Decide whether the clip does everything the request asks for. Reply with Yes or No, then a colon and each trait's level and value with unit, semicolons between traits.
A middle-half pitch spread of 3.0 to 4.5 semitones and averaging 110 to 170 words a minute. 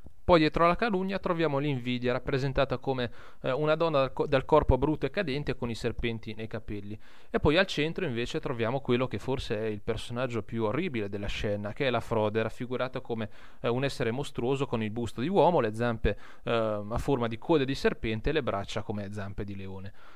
No: average, 4.1 semitones; fast, 210 wpm